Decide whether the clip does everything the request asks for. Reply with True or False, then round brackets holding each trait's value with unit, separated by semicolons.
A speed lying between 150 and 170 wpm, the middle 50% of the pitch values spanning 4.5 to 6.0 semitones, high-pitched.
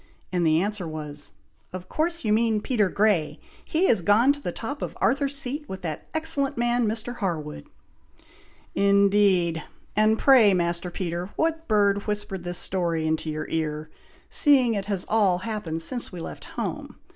True (165 wpm; 5.6 semitones; 200 Hz)